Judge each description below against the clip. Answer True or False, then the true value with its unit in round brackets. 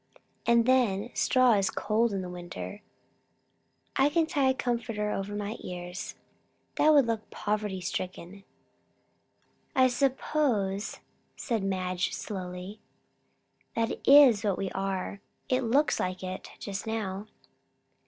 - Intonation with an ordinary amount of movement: True (4.3 semitones)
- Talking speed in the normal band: False (120 wpm)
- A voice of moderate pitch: False (210 Hz)